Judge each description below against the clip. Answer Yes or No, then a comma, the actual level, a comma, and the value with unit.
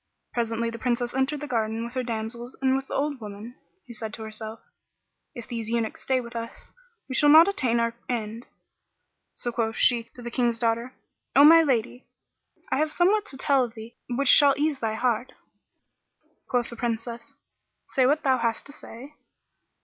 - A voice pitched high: Yes, high, 240 Hz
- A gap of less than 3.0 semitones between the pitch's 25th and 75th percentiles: Yes, narrow, 2.6 semitones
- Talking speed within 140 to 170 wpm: No, average, 180 wpm